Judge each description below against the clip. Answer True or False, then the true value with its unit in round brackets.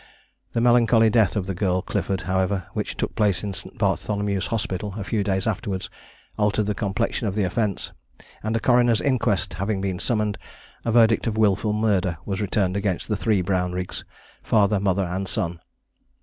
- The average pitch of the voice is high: False (100 Hz)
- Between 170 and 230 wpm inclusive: True (175 wpm)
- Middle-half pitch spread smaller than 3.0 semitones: True (2.5 semitones)